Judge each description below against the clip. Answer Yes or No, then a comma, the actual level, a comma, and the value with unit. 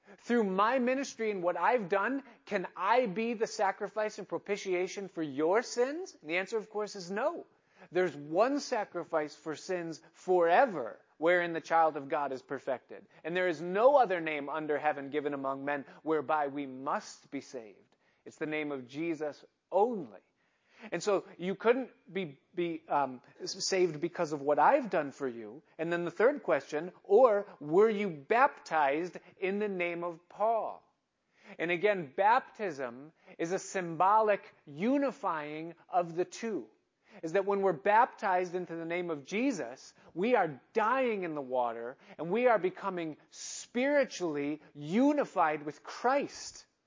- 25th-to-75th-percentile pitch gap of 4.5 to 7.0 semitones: Yes, average, 5.1 semitones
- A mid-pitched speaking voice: Yes, medium, 180 Hz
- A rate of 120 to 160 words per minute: Yes, average, 155 wpm